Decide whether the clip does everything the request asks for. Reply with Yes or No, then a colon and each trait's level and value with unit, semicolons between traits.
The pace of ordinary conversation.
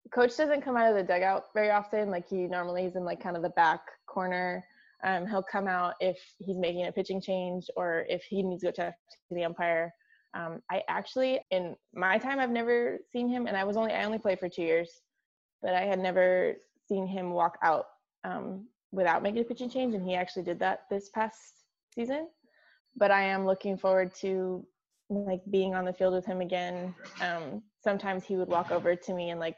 No: fast, 215 wpm